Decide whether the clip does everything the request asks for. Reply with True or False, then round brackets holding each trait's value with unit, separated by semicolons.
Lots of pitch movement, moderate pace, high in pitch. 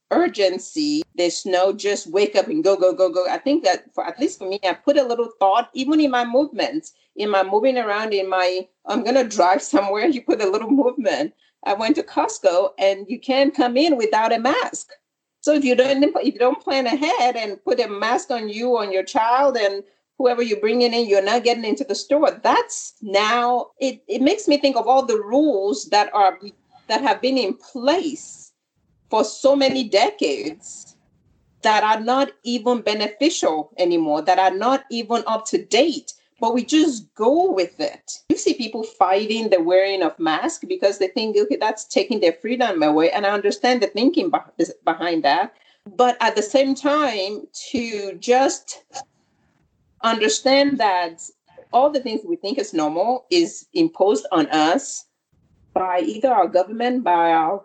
True (5.9 semitones; 180 wpm; 235 Hz)